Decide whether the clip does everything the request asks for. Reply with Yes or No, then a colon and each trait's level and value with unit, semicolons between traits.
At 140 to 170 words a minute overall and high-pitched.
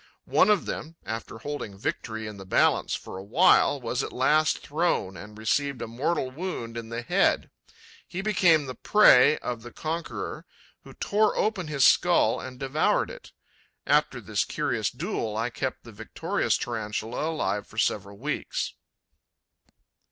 No: average, 155 wpm; low, 125 Hz